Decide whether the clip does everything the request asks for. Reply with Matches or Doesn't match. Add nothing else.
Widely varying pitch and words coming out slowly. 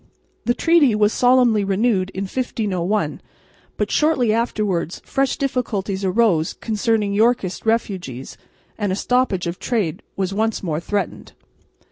Doesn't match